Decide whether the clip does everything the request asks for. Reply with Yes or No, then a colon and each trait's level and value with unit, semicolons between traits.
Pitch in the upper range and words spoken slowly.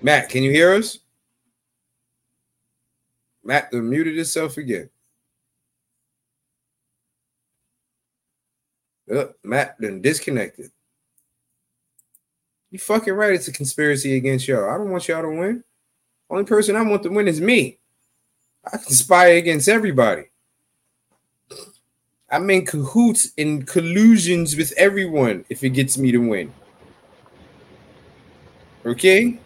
No: medium, 165 Hz; slow, 110 wpm